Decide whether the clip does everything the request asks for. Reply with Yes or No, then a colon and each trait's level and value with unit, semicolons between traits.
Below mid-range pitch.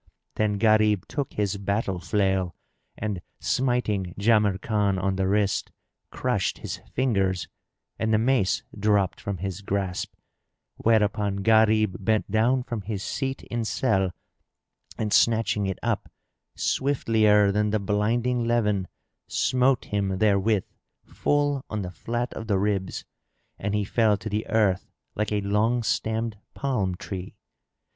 Yes: low, 105 Hz